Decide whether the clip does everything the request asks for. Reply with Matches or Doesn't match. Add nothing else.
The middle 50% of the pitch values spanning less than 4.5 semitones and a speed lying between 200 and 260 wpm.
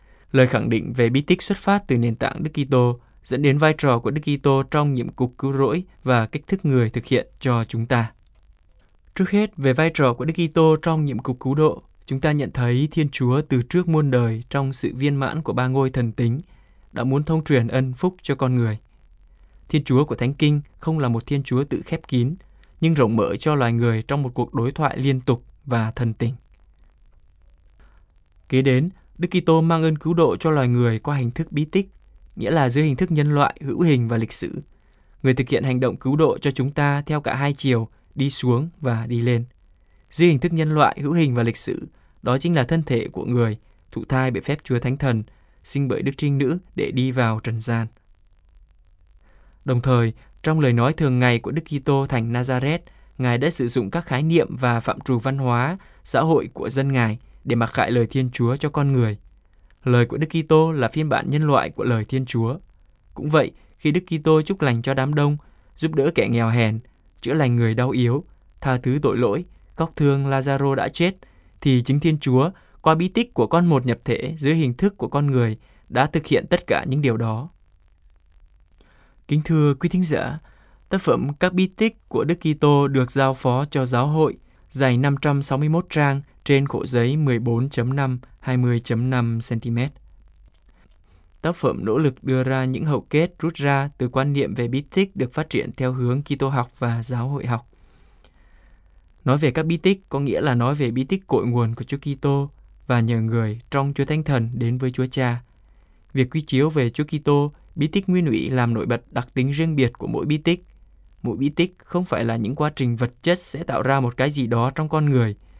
Matches